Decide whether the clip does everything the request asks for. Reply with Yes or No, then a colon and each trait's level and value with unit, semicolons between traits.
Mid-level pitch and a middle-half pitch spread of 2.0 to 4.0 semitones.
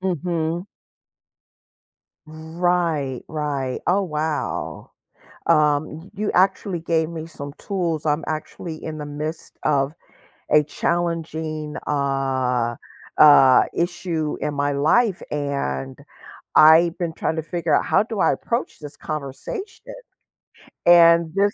Yes: medium, 160 Hz; average, 2.9 semitones